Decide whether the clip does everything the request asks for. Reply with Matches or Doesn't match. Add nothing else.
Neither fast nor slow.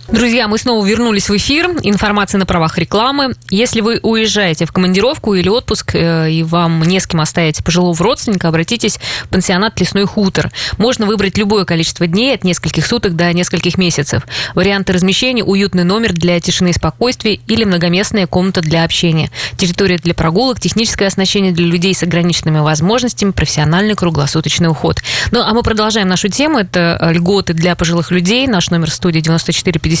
Doesn't match